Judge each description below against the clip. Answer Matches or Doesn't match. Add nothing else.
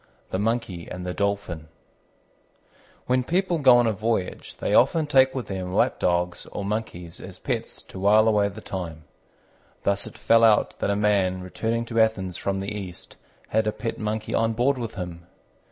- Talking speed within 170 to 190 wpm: Matches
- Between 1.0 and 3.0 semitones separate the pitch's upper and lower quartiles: Doesn't match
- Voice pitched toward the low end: Matches